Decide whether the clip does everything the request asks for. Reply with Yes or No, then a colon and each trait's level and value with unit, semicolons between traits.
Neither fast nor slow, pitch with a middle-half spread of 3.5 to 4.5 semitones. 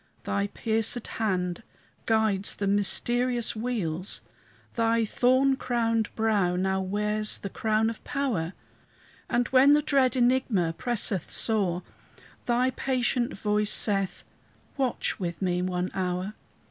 No: slow, 120 wpm; average, 4.2 semitones